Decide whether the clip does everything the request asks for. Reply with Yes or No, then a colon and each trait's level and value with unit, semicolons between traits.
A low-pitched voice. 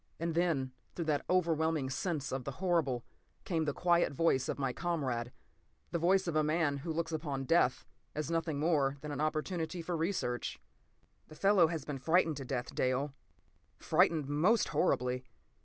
No: medium, 155 Hz